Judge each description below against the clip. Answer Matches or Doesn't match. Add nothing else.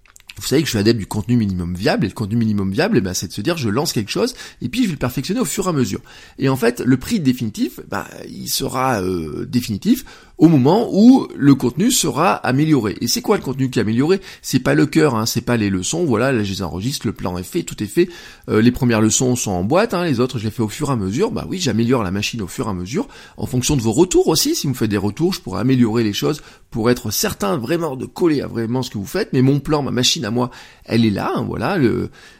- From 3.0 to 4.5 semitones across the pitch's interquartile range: Doesn't match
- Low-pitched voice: Matches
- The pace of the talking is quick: Matches